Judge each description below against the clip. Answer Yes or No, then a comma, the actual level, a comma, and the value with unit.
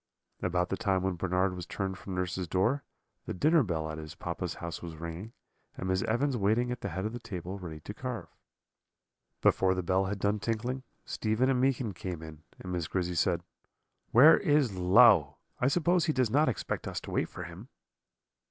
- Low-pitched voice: Yes, very low, 95 Hz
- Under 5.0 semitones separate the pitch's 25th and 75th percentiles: No, wide, 5.4 semitones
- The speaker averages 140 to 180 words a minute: No, average, 200 wpm